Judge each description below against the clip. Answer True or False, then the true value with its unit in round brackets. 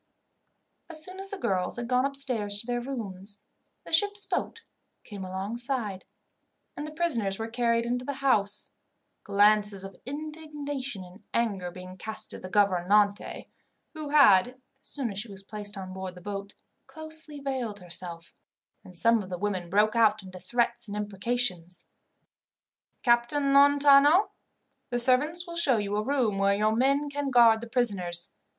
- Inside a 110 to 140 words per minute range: False (160 wpm)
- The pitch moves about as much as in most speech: False (5.8 semitones)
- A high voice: True (230 Hz)